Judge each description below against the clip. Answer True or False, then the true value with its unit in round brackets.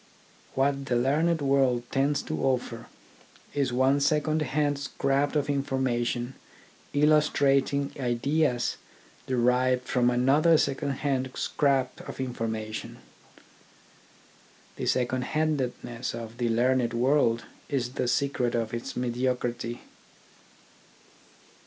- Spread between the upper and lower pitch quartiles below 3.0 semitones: True (2.6 semitones)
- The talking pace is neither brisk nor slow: False (100 wpm)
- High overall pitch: False (130 Hz)